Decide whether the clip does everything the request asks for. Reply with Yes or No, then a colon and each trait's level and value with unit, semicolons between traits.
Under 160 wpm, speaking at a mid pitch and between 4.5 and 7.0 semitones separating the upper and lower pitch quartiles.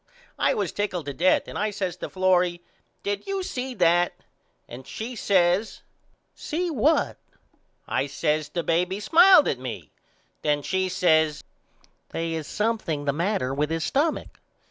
Yes: average, 150 wpm; medium, 180 Hz; average, 5.2 semitones